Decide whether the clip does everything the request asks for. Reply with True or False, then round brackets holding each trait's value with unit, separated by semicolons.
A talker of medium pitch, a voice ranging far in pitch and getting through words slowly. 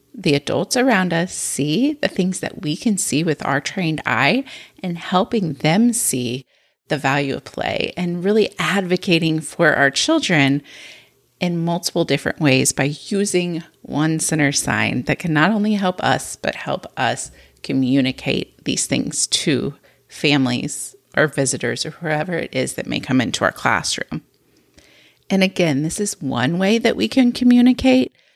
False (170 Hz; 6.0 semitones; 155 wpm)